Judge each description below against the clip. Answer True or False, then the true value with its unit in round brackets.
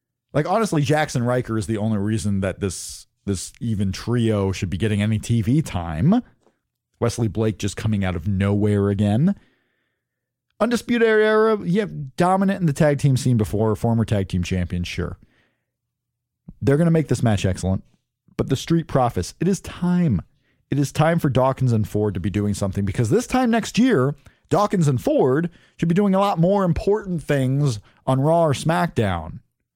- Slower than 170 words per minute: False (175 wpm)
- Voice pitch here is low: True (125 Hz)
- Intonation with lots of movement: True (8.0 semitones)